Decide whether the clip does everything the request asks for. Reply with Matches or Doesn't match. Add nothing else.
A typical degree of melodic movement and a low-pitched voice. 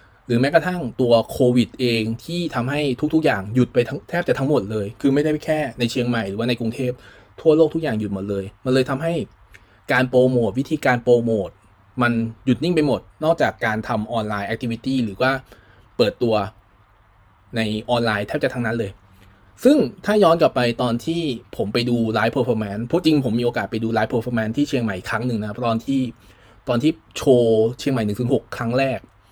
Matches